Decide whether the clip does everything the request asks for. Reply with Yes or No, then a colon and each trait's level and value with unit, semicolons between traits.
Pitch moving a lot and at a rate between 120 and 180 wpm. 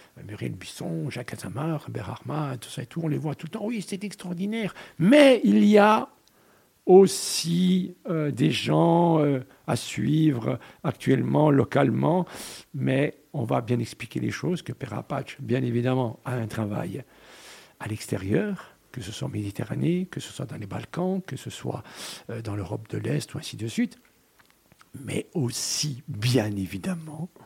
Yes: wide, 6.5 semitones; average, 165 wpm